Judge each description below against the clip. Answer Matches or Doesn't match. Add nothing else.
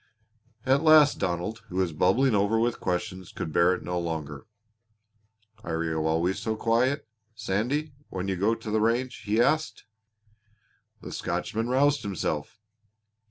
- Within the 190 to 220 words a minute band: Doesn't match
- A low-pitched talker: Matches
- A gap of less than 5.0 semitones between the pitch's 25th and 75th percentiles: Doesn't match